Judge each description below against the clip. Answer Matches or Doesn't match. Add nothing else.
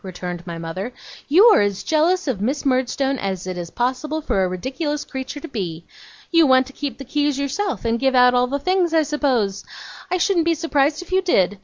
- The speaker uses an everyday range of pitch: Doesn't match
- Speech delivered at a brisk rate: Matches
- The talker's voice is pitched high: Matches